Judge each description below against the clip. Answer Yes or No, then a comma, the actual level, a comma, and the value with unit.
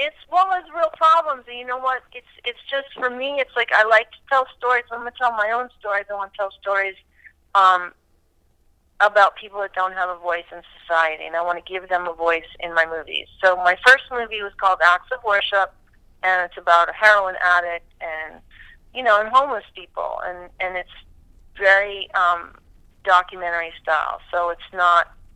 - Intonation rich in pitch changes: Yes, wide, 5.7 semitones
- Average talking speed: Yes, average, 195 wpm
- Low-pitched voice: No, high, 190 Hz